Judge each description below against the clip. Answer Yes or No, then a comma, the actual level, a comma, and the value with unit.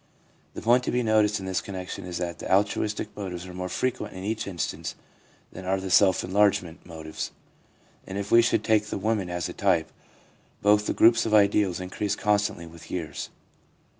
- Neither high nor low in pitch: No, low, 100 Hz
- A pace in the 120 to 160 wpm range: No, average, 190 wpm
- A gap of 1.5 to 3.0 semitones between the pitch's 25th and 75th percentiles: Yes, average, 2.7 semitones